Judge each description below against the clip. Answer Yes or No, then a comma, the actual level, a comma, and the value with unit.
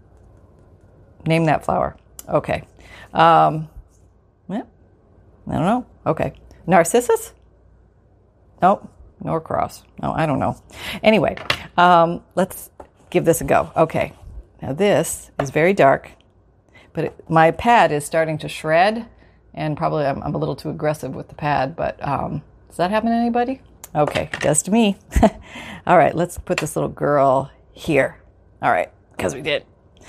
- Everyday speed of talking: Yes, average, 150 wpm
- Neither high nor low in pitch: Yes, medium, 160 Hz